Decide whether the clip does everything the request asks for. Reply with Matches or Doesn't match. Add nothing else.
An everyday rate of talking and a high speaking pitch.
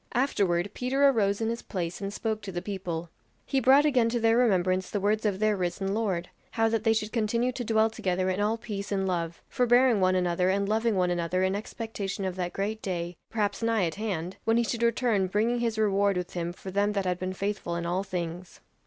Doesn't match